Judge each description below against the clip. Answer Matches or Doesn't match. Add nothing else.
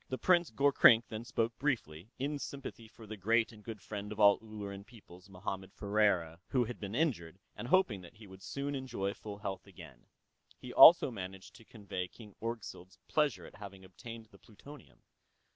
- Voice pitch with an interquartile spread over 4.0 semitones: Doesn't match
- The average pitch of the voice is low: Matches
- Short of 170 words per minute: Doesn't match